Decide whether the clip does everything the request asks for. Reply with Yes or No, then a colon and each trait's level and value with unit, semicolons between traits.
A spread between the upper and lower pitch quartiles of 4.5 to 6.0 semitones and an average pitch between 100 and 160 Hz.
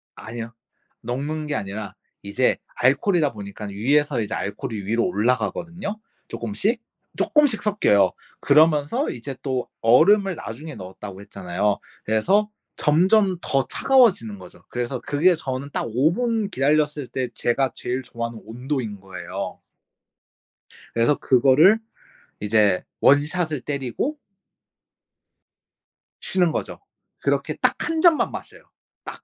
No: wide, 7.3 semitones; low, 135 Hz